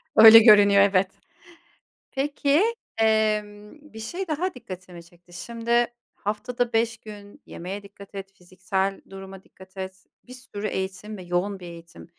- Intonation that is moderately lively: Yes, average, 3.1 semitones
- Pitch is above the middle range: Yes, high, 205 Hz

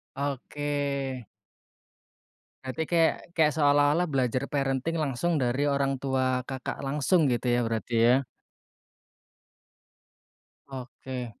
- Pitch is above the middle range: No, low, 135 Hz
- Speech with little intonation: Yes, narrow, 2.1 semitones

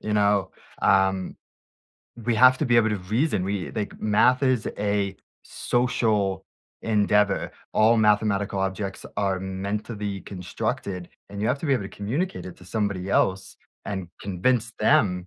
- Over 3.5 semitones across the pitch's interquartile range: No, narrow, 2.6 semitones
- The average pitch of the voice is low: Yes, low, 105 Hz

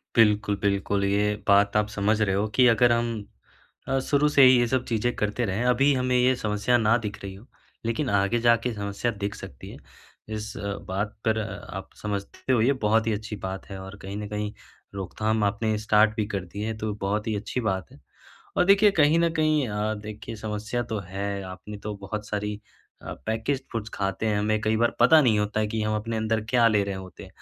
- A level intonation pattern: Yes, narrow, 2.3 semitones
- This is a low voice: Yes, low, 110 Hz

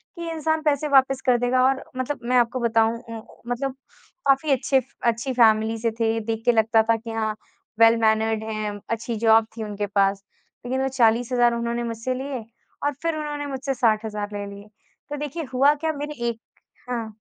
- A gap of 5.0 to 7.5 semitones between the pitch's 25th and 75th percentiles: No, average, 3.3 semitones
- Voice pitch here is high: Yes, high, 235 Hz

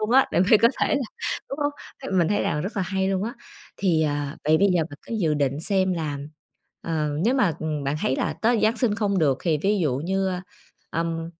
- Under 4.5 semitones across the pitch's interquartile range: No, average, 5.1 semitones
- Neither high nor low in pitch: Yes, medium, 180 Hz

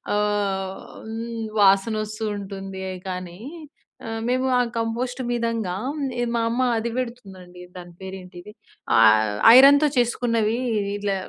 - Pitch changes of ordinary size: Yes, average, 3.6 semitones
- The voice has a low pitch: No, high, 210 Hz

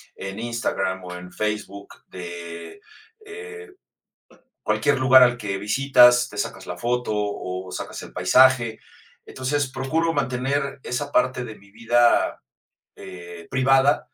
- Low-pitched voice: Yes, low, 120 Hz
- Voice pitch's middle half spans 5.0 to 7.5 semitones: Yes, wide, 5.4 semitones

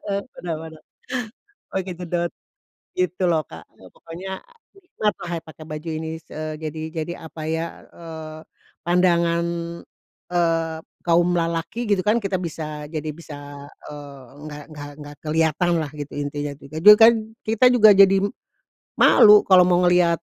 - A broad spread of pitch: No, narrow, 2.6 semitones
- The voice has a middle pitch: Yes, medium, 165 Hz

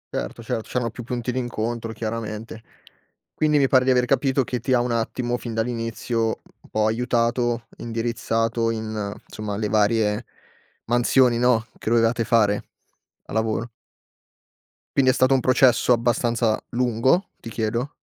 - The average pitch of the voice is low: Yes, low, 115 Hz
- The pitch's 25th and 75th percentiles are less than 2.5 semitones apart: Yes, narrow, 1.6 semitones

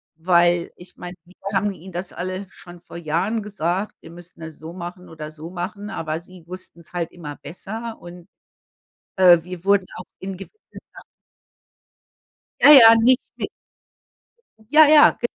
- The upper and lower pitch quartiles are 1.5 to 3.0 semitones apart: Yes, narrow, 2.6 semitones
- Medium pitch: Yes, medium, 180 Hz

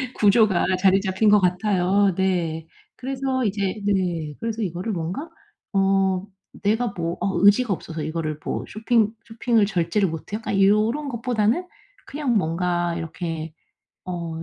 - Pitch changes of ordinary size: Yes, average, 4.1 semitones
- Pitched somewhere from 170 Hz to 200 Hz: Yes, high, 195 Hz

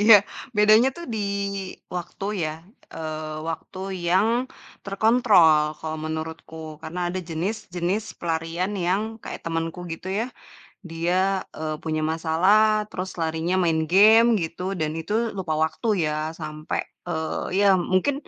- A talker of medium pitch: Yes, medium, 170 Hz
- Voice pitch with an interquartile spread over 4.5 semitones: No, average, 4.1 semitones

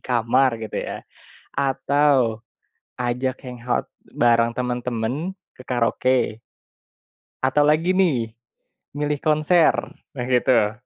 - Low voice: Yes, low, 125 Hz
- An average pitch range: Yes, average, 3.6 semitones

